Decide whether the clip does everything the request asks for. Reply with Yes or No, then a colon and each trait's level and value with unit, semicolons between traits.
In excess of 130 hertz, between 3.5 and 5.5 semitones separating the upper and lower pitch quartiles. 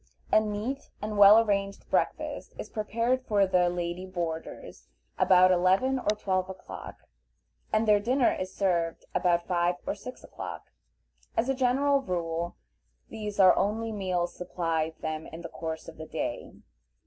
Yes: high, 190 Hz; average, 3.8 semitones